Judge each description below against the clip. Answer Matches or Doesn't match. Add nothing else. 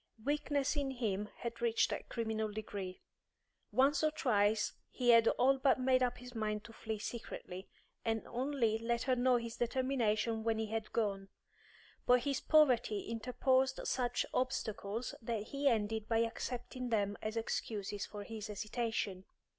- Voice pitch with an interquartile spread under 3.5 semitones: Matches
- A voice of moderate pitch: Doesn't match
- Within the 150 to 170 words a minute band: Matches